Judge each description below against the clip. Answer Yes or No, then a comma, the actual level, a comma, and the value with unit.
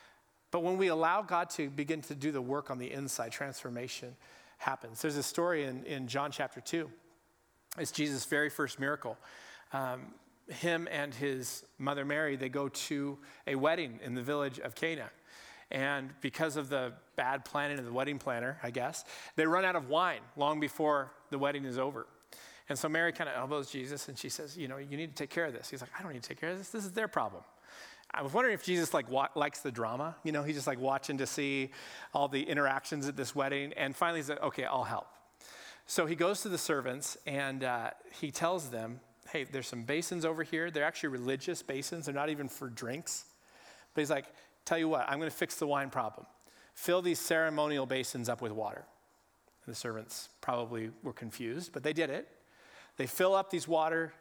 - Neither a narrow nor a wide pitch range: Yes, average, 3.3 semitones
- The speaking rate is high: Yes, fast, 215 wpm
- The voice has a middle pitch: Yes, medium, 145 Hz